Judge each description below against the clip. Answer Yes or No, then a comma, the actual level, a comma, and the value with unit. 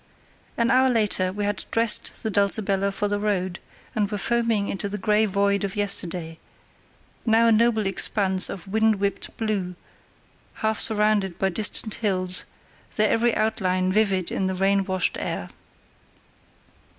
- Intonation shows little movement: Yes, narrow, 2.3 semitones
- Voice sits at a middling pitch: No, high, 205 Hz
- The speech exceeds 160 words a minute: No, average, 150 wpm